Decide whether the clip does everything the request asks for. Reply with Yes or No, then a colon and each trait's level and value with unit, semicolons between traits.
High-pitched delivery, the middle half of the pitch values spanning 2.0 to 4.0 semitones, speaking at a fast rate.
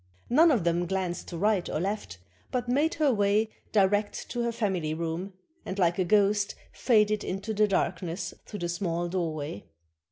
No: high, 195 Hz; average, 3.7 semitones; average, 180 wpm